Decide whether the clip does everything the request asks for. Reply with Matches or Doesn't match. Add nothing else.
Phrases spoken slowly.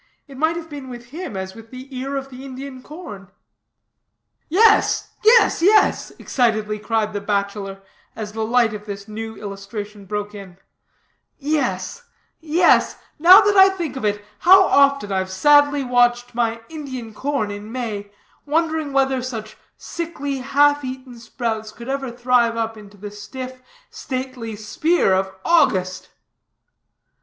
Doesn't match